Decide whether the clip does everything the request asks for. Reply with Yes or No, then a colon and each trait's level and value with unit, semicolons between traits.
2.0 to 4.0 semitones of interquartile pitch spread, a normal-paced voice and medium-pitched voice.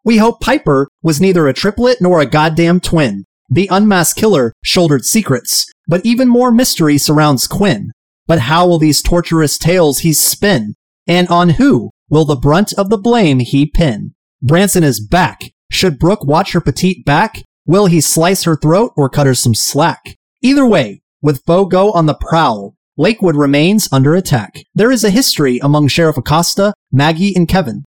No: average, 4.9 semitones; average, 175 wpm; medium, 170 Hz